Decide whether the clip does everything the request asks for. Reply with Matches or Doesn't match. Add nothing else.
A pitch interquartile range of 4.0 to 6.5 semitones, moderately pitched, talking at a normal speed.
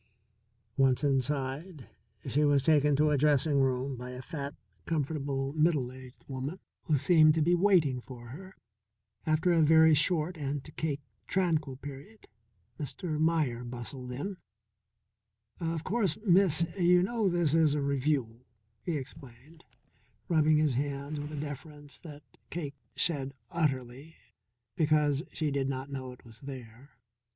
Doesn't match